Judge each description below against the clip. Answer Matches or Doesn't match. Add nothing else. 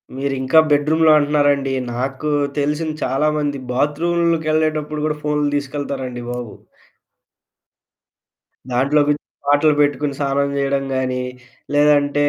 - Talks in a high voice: Doesn't match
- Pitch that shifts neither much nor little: Doesn't match